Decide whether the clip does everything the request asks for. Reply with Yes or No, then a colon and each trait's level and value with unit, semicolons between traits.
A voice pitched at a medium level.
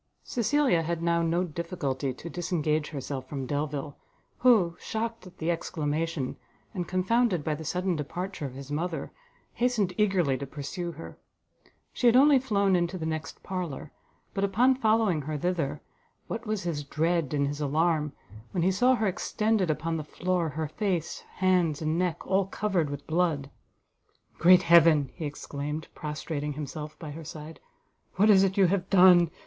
Yes: medium, 170 Hz